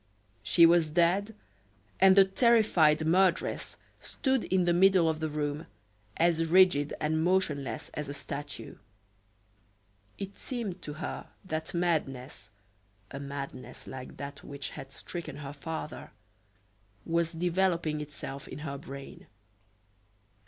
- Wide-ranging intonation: No, average, 4.0 semitones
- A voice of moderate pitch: Yes, medium, 160 Hz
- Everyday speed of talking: No, slow, 125 wpm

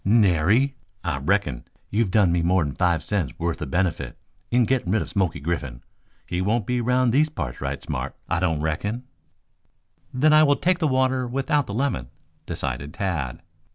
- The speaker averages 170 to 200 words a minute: Yes, average, 175 wpm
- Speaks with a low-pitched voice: Yes, very low, 95 Hz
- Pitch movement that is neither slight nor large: No, wide, 8.1 semitones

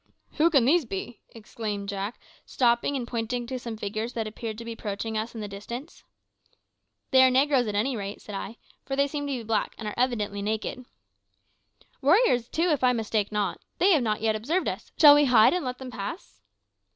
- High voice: Yes, high, 235 Hz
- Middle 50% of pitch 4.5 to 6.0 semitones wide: No, average, 3.6 semitones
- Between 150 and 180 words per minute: No, fast, 205 wpm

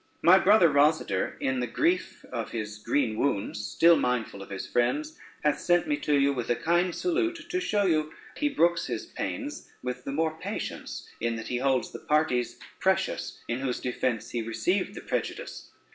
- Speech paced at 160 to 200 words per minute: Yes, average, 185 wpm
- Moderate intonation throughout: No, wide, 6.7 semitones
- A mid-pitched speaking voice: Yes, medium, 145 Hz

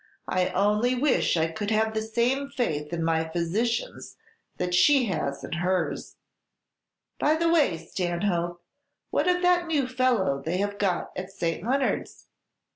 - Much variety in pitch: Yes, wide, 6.9 semitones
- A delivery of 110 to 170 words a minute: Yes, average, 150 wpm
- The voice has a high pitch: Yes, high, 205 Hz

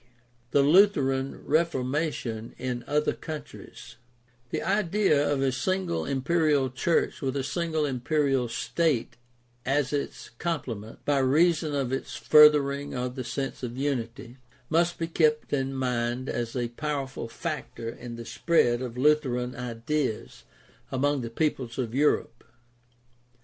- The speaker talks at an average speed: No, slow, 130 wpm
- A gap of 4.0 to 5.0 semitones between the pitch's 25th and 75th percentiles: No, average, 3.6 semitones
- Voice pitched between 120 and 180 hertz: Yes, low, 135 Hz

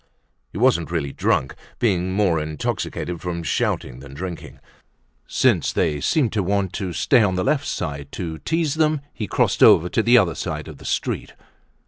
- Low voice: Yes, very low, 90 Hz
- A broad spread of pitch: Yes, wide, 5.8 semitones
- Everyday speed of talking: Yes, average, 180 wpm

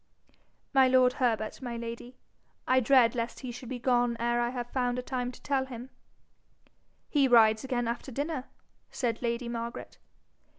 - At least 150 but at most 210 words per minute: Yes, average, 165 wpm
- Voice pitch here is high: Yes, high, 245 Hz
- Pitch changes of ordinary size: No, narrow, 1.7 semitones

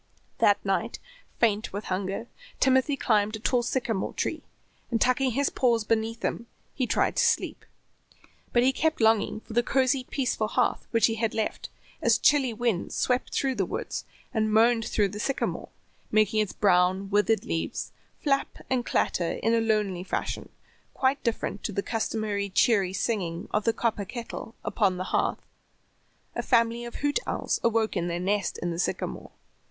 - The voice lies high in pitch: Yes, high, 225 Hz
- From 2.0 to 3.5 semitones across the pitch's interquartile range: Yes, average, 3.0 semitones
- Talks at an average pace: Yes, average, 170 wpm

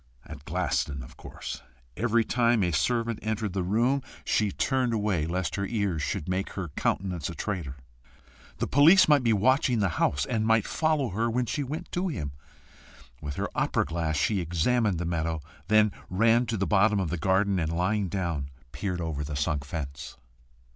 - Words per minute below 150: No, average, 180 wpm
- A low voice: Yes, low, 100 Hz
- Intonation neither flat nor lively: No, wide, 5.8 semitones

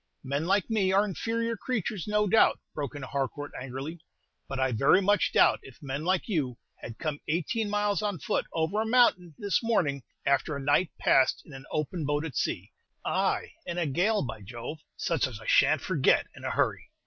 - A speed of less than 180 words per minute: No, fast, 205 wpm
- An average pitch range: No, wide, 6.8 semitones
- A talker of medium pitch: Yes, medium, 160 Hz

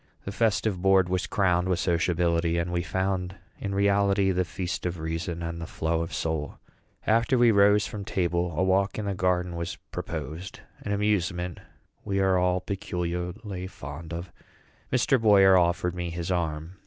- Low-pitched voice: Yes, very low, 90 Hz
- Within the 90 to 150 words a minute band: No, average, 165 wpm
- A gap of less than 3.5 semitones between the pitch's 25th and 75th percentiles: Yes, narrow, 2.4 semitones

